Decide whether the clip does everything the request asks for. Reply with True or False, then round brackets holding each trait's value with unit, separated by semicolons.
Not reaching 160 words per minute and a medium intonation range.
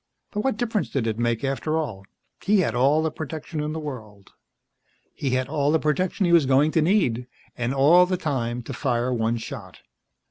False (200 wpm; 5.0 semitones)